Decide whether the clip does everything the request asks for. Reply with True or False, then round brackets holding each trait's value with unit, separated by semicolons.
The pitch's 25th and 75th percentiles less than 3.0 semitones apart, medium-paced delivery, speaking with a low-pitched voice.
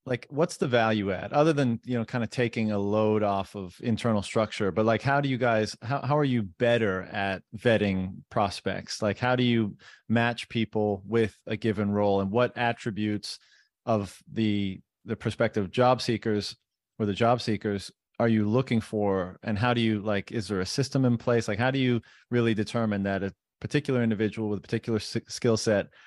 True (2.6 semitones; 195 wpm; 110 Hz)